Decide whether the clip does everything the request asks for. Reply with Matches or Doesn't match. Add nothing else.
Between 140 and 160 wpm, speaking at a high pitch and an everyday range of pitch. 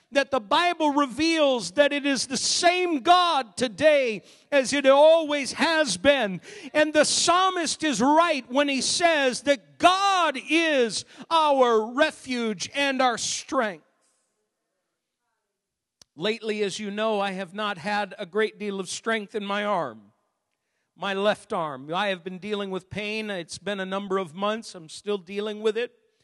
Doesn't match